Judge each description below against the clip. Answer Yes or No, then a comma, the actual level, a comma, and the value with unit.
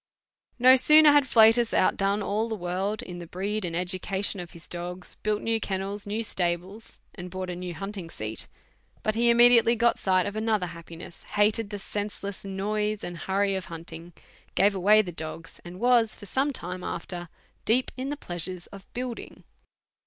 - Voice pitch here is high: Yes, high, 200 Hz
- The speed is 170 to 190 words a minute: Yes, average, 175 wpm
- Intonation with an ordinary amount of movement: Yes, average, 3.6 semitones